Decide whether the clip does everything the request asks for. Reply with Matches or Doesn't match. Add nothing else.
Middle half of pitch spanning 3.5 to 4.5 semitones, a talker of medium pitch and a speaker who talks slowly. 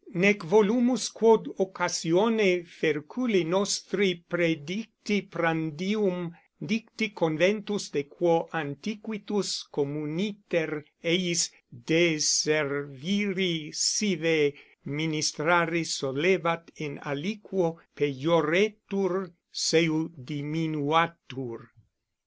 Matches